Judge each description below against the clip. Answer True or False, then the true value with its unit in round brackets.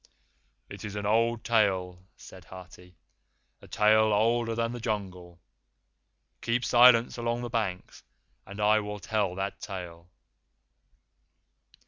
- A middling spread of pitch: True (3.7 semitones)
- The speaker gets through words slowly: True (120 wpm)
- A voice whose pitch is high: False (105 Hz)